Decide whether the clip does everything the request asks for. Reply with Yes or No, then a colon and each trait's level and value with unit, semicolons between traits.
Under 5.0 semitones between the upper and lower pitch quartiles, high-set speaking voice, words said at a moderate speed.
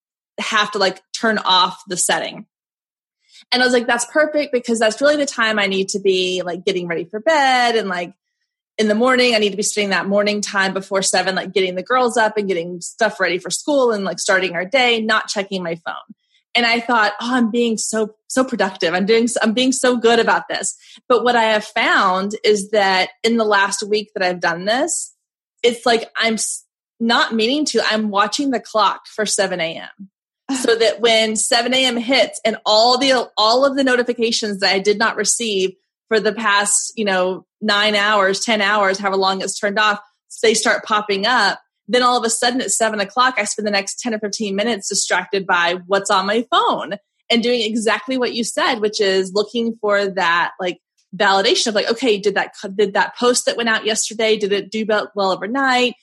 No: average, 3.2 semitones; high, 215 Hz; fast, 210 wpm